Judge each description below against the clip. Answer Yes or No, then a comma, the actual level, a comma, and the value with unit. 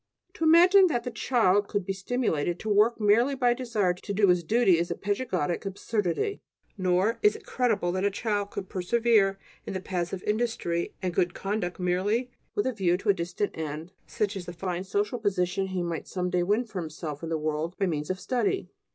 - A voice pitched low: No, high, 195 Hz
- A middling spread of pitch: Yes, average, 4.3 semitones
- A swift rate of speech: Yes, fast, 210 wpm